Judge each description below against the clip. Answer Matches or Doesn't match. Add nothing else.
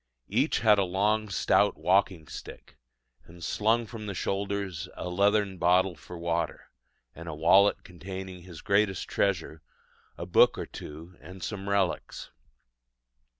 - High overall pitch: Doesn't match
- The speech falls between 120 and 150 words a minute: Matches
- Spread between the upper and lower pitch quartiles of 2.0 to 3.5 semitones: Matches